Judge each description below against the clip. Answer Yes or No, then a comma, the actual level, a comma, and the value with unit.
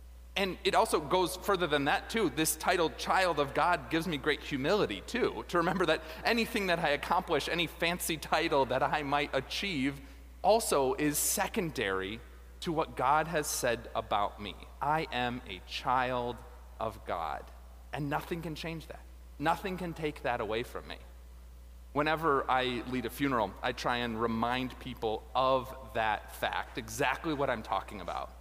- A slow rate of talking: No, average, 165 wpm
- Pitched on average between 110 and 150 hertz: Yes, low, 135 Hz